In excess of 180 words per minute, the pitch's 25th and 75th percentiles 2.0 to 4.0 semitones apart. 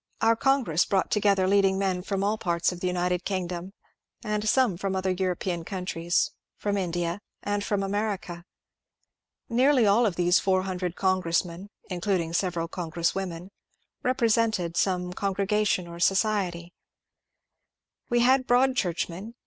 No: slow, 135 wpm; average, 2.9 semitones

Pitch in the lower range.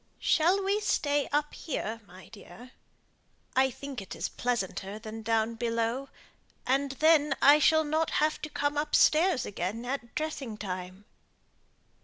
No: very high, 265 Hz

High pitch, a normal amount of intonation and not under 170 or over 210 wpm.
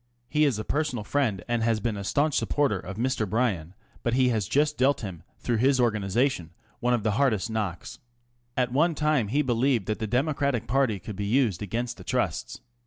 No: low, 120 Hz; average, 4.6 semitones; fast, 205 wpm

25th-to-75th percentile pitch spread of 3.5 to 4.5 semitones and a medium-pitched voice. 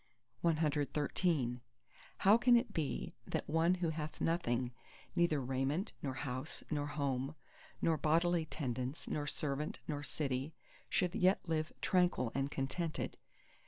Yes: average, 3.8 semitones; medium, 150 Hz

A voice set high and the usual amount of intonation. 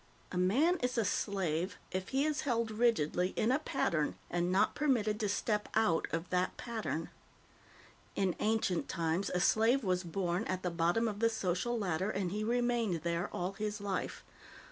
Yes: high, 200 Hz; average, 4.3 semitones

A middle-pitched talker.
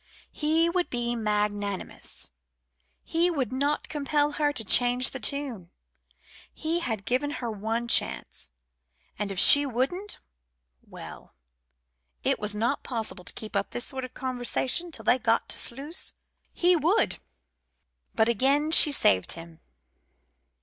No: very high, 255 Hz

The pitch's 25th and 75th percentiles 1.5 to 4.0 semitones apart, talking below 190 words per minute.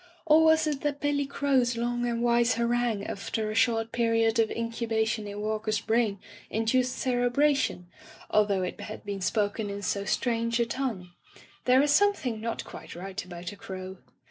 Yes: average, 2.9 semitones; average, 170 wpm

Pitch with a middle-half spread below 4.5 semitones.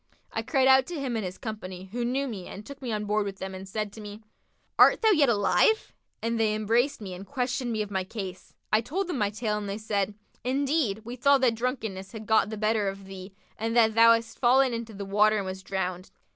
Yes: average, 3.7 semitones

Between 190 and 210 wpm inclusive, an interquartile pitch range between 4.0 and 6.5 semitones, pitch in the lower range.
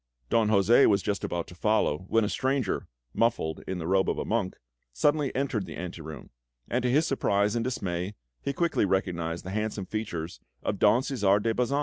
Yes: average, 200 wpm; average, 4.8 semitones; low, 105 Hz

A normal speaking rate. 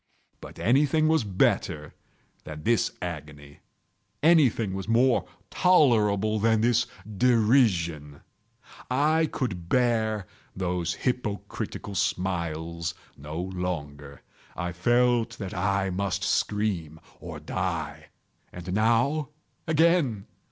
No: slow, 95 wpm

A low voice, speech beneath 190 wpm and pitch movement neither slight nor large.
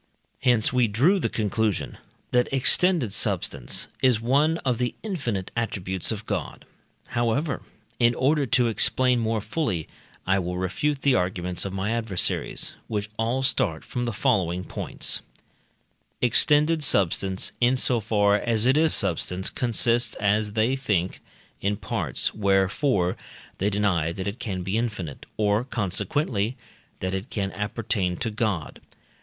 Yes: low, 110 Hz; average, 140 wpm; average, 4.5 semitones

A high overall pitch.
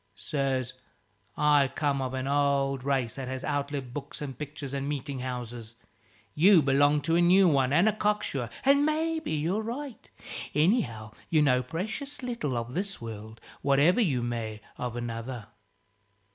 No: medium, 140 Hz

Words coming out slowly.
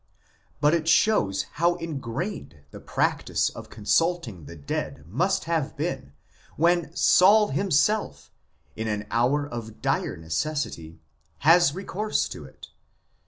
Yes: slow, 120 wpm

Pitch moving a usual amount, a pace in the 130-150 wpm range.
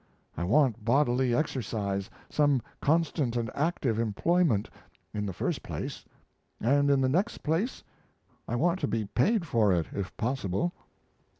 No: wide, 5.9 semitones; average, 140 wpm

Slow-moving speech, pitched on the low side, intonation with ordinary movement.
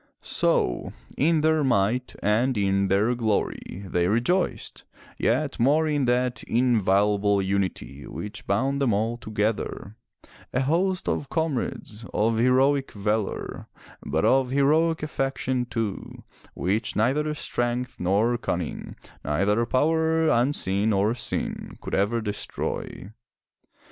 Yes: slow, 115 wpm; low, 120 Hz; average, 4.9 semitones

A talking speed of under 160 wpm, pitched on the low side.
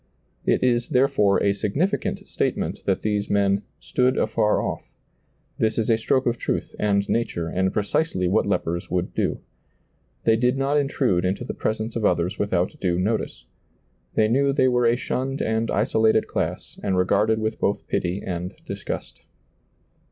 No: average, 165 wpm; low, 110 Hz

